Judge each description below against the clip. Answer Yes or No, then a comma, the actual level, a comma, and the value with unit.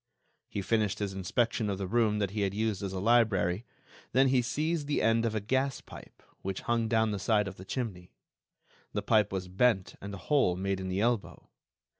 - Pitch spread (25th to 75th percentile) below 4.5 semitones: Yes, average, 3.6 semitones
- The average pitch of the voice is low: Yes, low, 105 Hz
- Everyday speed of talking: No, fast, 210 wpm